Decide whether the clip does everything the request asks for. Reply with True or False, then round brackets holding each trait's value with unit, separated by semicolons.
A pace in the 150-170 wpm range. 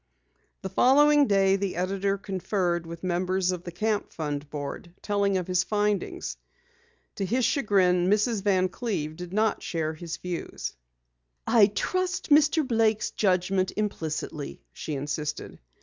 False (135 wpm)